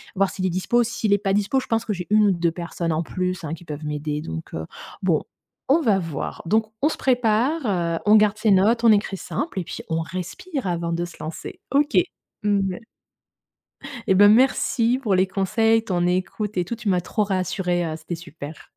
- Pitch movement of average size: Yes, average, 4.4 semitones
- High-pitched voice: Yes, high, 195 Hz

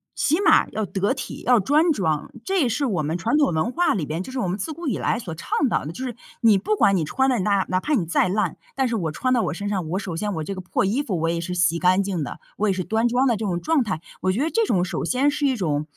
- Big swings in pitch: Yes, wide, 6.4 semitones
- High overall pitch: Yes, high, 205 Hz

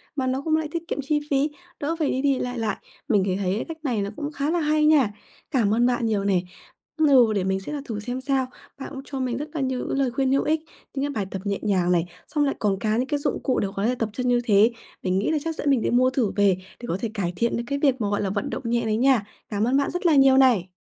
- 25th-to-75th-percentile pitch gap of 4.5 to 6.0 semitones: Yes, average, 5.2 semitones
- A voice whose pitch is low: No, very high, 250 Hz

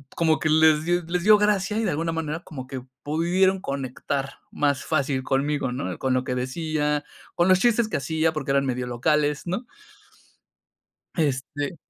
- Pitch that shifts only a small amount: No, average, 3.9 semitones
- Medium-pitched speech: Yes, medium, 150 Hz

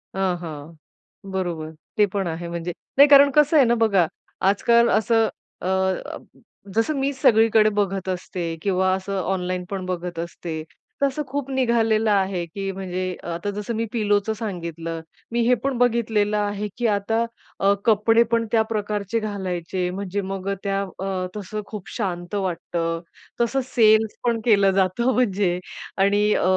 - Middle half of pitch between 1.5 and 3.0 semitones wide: No, average, 3.6 semitones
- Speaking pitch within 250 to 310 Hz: No, high, 200 Hz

